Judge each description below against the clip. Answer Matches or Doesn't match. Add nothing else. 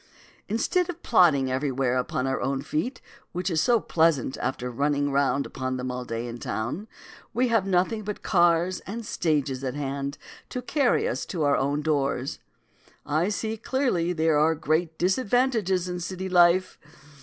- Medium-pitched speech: Matches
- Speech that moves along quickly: Doesn't match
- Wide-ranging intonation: Matches